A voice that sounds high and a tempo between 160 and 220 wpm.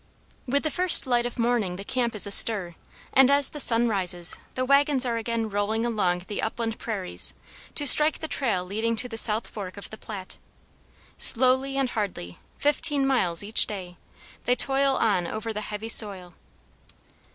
Yes: high, 225 Hz; average, 175 wpm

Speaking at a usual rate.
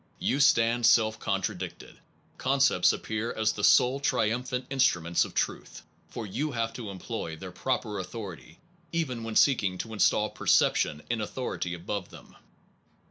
Yes: average, 145 wpm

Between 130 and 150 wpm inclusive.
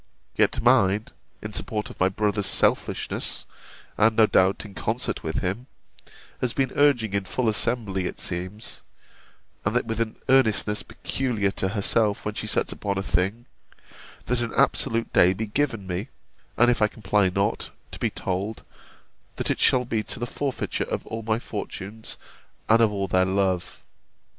No: average, 165 wpm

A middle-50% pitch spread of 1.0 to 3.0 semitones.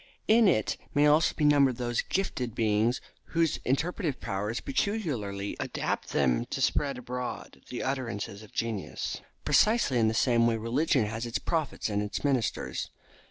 No: average, 5.0 semitones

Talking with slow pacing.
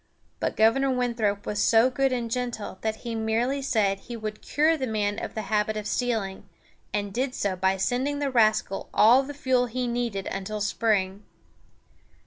No: average, 175 wpm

